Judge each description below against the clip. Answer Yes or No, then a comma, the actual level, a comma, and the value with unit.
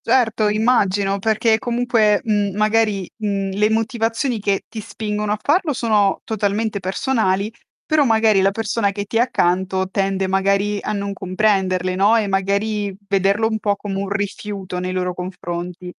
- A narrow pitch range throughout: Yes, narrow, 2.3 semitones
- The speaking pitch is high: Yes, high, 205 Hz